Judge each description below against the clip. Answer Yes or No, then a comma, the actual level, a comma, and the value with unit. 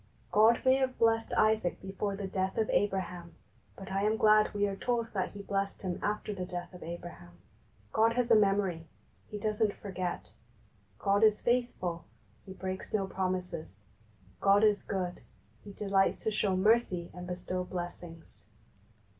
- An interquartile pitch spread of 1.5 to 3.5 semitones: Yes, average, 2.8 semitones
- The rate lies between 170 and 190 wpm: No, average, 160 wpm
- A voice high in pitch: Yes, high, 195 Hz